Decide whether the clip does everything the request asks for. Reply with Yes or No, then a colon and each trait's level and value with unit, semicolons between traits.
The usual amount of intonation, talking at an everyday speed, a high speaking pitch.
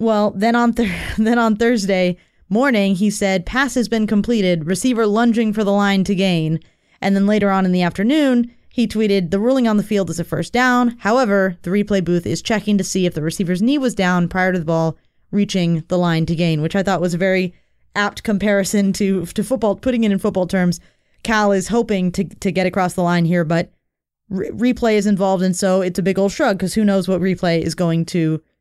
No: average, 3.2 semitones; fast, 225 wpm; high, 195 Hz